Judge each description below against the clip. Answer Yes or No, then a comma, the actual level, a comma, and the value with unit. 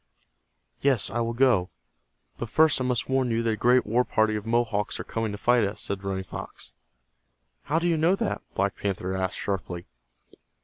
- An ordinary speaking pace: Yes, average, 190 wpm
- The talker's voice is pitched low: Yes, low, 115 Hz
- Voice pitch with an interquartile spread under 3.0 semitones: No, average, 4.1 semitones